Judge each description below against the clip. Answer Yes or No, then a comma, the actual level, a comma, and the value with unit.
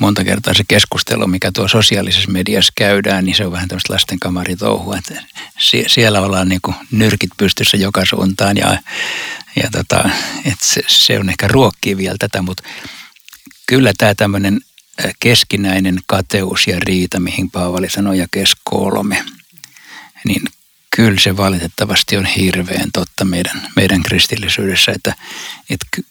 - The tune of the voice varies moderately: No, narrow, 1.7 semitones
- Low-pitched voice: Yes, very low, 95 Hz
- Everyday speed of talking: Yes, average, 145 wpm